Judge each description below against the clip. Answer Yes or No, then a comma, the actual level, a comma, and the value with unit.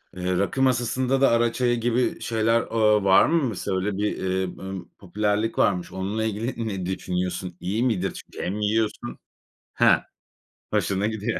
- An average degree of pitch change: Yes, average, 3.5 semitones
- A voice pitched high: No, low, 105 Hz